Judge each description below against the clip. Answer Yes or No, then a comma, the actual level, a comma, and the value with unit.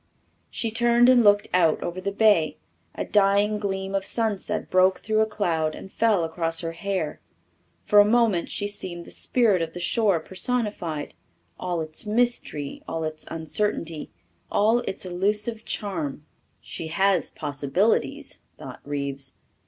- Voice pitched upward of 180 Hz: Yes, high, 190 Hz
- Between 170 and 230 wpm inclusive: No, average, 145 wpm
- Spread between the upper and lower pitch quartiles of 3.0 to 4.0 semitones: No, average, 4.4 semitones